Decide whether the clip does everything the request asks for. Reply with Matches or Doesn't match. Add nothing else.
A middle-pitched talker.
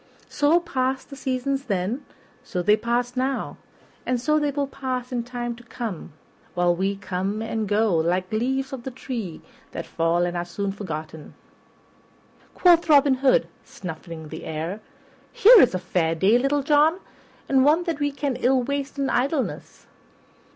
Doesn't match